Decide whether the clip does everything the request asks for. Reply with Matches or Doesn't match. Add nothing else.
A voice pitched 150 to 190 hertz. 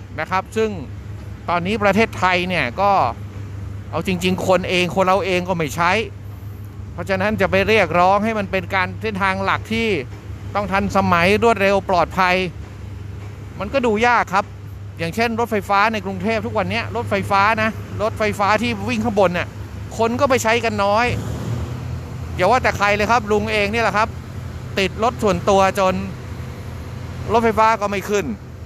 Matches